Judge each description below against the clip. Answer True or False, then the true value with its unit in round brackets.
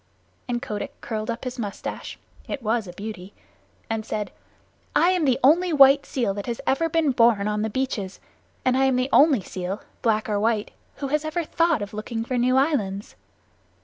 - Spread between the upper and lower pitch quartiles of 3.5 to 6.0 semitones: True (4.5 semitones)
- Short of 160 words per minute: False (185 wpm)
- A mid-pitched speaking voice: False (240 Hz)